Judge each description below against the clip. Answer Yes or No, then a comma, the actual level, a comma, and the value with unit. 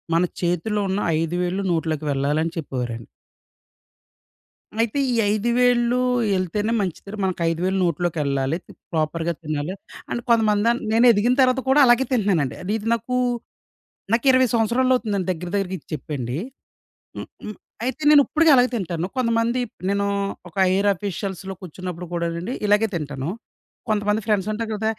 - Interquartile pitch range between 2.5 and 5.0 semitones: No, wide, 5.5 semitones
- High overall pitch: Yes, high, 195 Hz